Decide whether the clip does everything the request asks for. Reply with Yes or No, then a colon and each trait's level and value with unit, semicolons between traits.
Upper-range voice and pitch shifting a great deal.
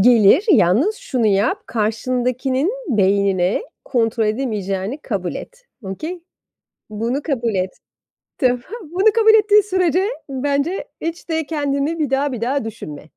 Yes: very high, 255 Hz; wide, 7.1 semitones